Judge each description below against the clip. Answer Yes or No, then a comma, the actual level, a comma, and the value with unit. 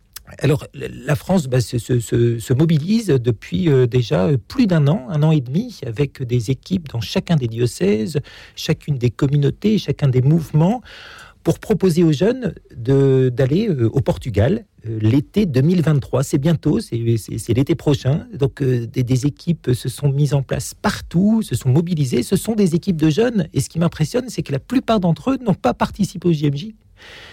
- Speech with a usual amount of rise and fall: No, wide, 5.8 semitones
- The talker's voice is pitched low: No, medium, 150 Hz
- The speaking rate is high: No, average, 180 wpm